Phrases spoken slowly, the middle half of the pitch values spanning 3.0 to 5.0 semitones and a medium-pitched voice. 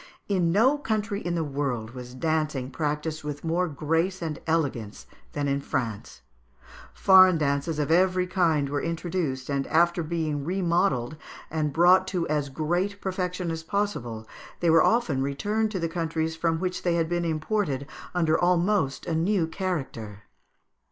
No: average, 155 wpm; average, 3.9 semitones; medium, 165 Hz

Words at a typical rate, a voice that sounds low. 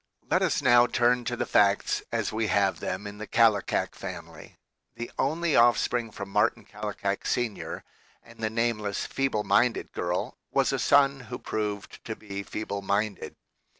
Yes: average, 160 wpm; low, 110 Hz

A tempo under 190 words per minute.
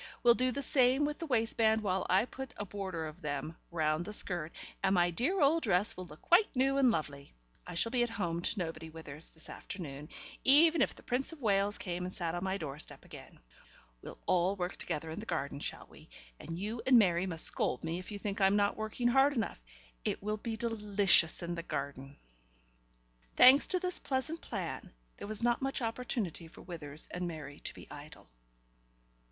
No: fast, 205 wpm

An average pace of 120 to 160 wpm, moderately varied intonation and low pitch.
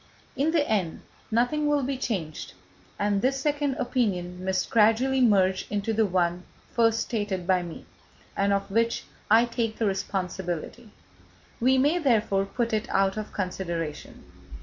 No: average, 150 wpm; average, 4.5 semitones; high, 215 Hz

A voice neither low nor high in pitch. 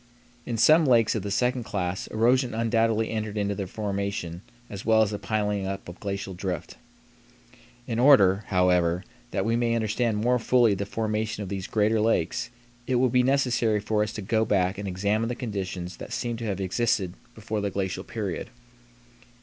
No: low, 105 Hz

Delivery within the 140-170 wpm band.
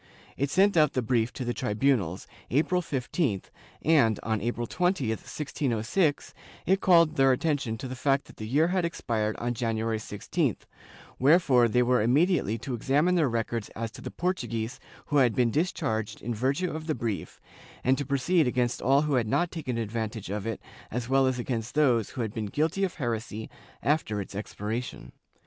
No: average, 180 wpm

